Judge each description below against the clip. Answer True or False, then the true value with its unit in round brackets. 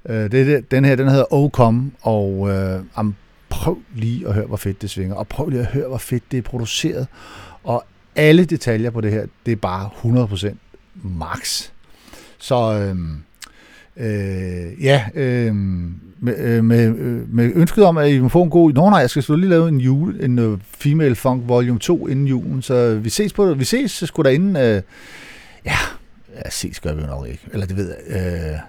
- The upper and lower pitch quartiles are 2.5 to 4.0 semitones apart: False (5.5 semitones)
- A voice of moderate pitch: False (120 Hz)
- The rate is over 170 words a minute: True (205 wpm)